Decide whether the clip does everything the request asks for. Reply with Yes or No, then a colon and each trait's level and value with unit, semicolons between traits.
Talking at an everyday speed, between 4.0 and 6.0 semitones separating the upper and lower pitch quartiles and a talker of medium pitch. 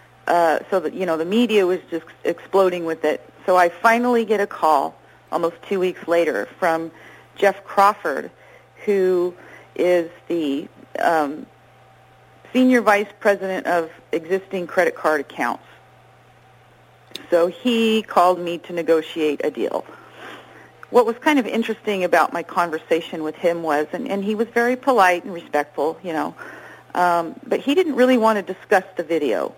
Yes: average, 155 wpm; average, 4.3 semitones; medium, 180 Hz